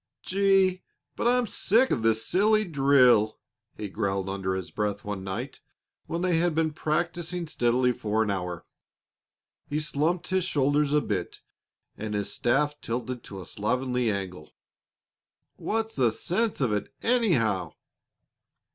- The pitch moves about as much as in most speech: No, wide, 8.7 semitones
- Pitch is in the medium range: No, low, 130 Hz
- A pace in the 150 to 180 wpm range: No, average, 140 wpm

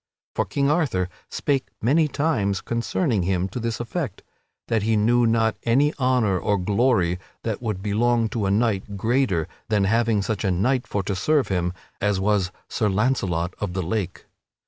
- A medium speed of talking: Yes, average, 170 wpm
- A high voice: No, low, 110 Hz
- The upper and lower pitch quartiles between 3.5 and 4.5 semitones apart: Yes, average, 3.9 semitones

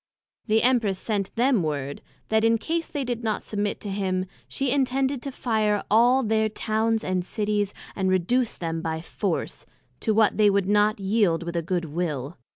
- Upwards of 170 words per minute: Yes, average, 180 wpm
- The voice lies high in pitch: Yes, high, 210 Hz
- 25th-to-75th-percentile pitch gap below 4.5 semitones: Yes, average, 3.7 semitones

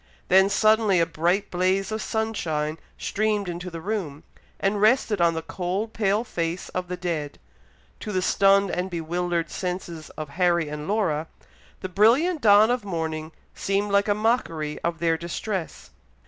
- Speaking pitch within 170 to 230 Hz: Yes, medium, 185 Hz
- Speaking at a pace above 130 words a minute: Yes, average, 160 wpm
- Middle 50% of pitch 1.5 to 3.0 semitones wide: No, average, 3.9 semitones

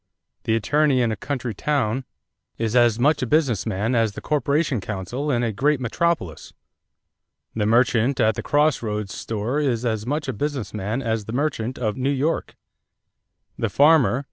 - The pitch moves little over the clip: No, average, 4.5 semitones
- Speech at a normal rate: Yes, average, 170 wpm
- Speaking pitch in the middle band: No, low, 120 Hz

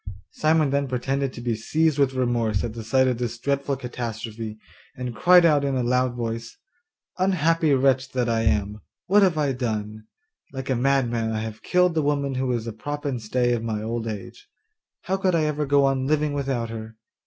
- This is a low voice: Yes, low, 130 Hz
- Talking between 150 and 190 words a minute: No, average, 200 wpm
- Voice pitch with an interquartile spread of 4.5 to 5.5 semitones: No, average, 3.8 semitones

